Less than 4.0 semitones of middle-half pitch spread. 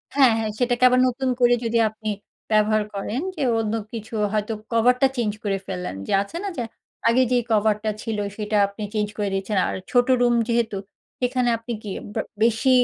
Yes: narrow, 2.5 semitones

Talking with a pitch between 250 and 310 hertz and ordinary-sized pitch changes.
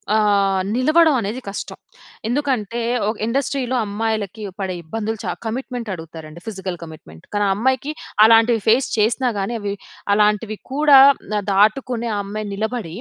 No: high, 220 Hz; average, 3.6 semitones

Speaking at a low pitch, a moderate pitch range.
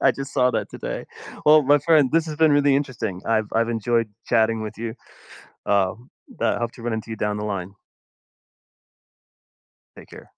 Yes: low, 115 Hz; average, 4.4 semitones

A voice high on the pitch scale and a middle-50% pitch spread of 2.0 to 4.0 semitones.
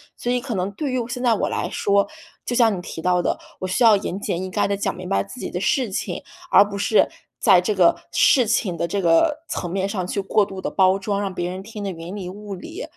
Yes: high, 195 Hz; average, 3.2 semitones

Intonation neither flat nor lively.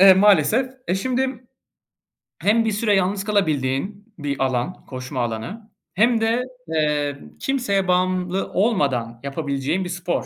No: wide, 6.9 semitones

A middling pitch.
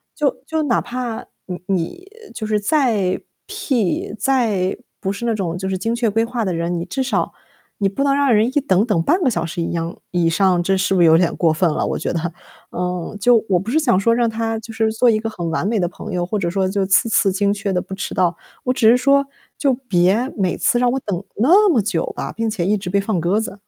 No: high, 205 Hz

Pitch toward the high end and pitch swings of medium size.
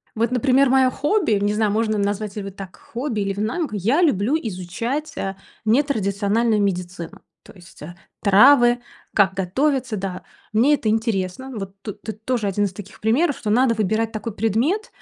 Yes: high, 215 Hz; average, 4.3 semitones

